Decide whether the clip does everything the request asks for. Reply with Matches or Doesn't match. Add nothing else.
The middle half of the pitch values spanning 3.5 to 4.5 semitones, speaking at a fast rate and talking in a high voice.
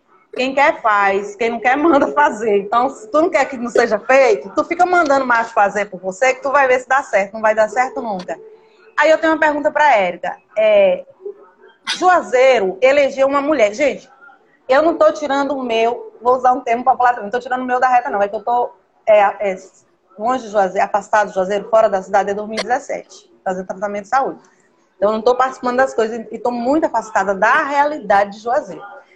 Doesn't match